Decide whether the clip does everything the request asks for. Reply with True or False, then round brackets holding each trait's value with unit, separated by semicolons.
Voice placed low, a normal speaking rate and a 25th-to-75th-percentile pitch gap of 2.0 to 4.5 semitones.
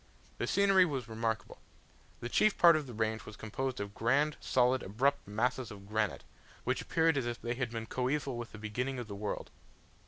True (120 Hz; 195 wpm; 3.7 semitones)